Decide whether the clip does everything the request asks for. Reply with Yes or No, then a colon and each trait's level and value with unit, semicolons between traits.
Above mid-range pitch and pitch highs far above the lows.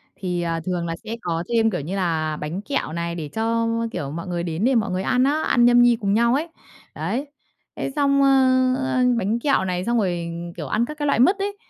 Yes: high, 210 Hz; wide, 6.7 semitones